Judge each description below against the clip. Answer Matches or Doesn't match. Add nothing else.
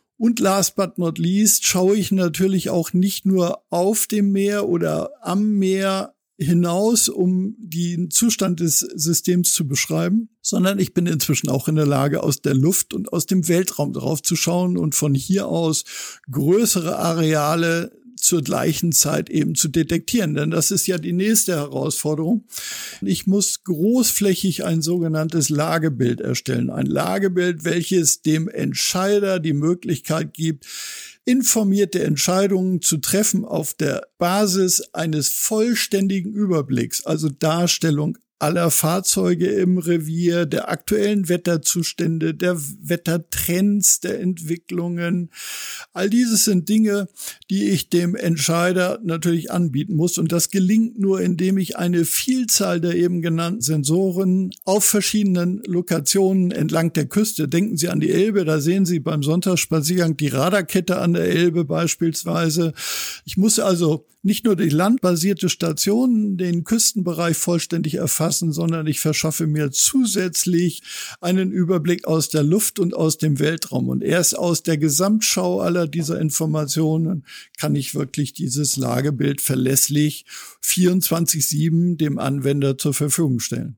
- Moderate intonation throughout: Matches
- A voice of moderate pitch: Matches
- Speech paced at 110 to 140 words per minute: Matches